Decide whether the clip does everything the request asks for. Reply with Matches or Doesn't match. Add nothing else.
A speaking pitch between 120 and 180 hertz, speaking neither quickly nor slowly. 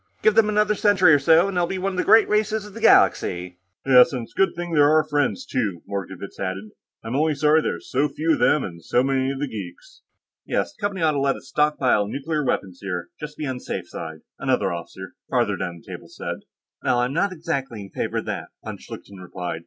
Doesn't match